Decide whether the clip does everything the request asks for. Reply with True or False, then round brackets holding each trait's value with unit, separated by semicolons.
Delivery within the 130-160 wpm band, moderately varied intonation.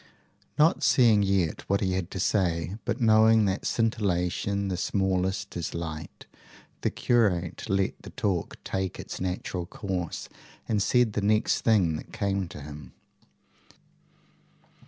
True (135 wpm; 3.1 semitones)